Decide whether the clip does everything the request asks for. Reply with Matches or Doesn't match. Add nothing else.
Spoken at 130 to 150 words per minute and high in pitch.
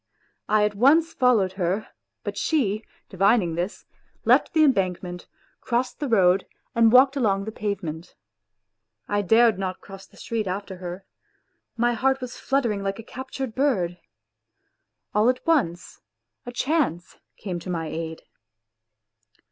Matches